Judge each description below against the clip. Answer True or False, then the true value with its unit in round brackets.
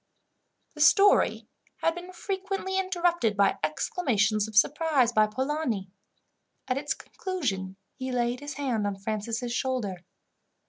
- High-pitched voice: True (255 Hz)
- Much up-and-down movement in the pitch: True (7.5 semitones)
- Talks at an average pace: False (125 wpm)